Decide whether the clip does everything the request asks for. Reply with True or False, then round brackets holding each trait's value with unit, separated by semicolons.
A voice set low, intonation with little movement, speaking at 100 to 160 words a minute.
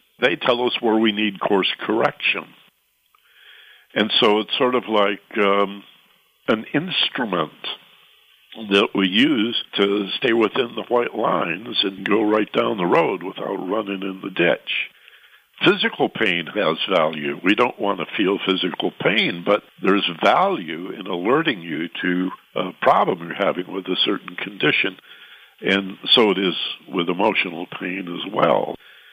True (100 Hz; 2.2 semitones; 150 wpm)